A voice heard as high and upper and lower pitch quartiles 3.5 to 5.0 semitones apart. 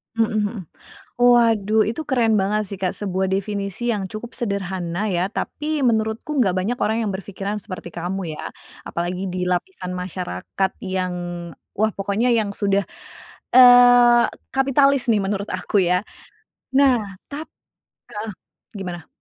Yes: high, 205 Hz; average, 4.1 semitones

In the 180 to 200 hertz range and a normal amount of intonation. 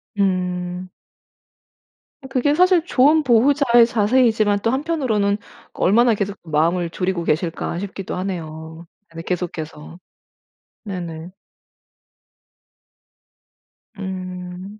Yes: high, 190 Hz; average, 5.0 semitones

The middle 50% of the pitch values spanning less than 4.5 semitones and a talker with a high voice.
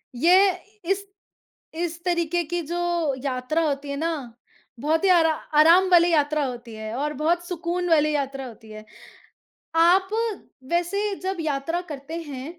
Yes: average, 3.9 semitones; very high, 325 Hz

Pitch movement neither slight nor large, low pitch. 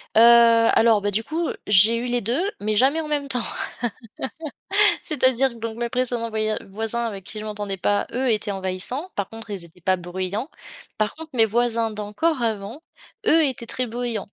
No: average, 3.3 semitones; high, 225 Hz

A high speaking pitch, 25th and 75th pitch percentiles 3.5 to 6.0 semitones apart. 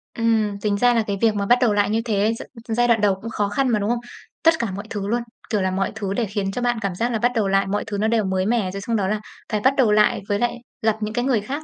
No: high, 215 Hz; narrow, 2.6 semitones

